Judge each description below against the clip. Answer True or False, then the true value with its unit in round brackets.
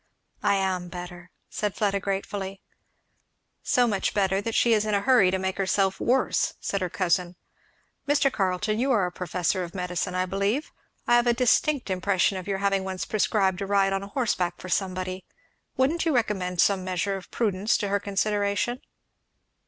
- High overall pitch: True (195 Hz)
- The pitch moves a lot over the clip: False (2.4 semitones)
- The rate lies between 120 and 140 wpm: False (175 wpm)